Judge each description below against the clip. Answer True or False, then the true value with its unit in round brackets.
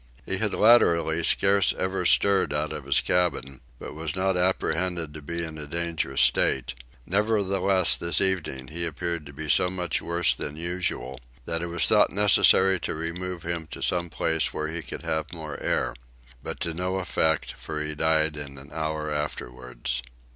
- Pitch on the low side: True (85 Hz)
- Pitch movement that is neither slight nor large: True (3.1 semitones)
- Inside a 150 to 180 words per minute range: True (175 wpm)